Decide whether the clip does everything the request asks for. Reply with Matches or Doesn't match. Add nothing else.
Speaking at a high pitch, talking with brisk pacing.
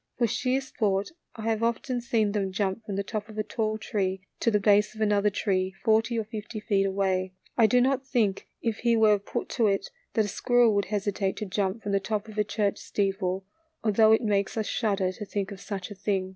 Matches